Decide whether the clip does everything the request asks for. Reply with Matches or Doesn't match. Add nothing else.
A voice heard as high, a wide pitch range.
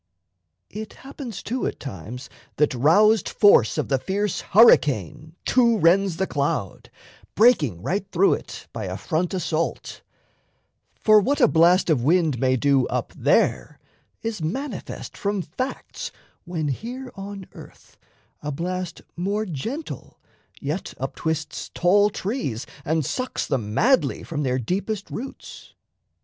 Doesn't match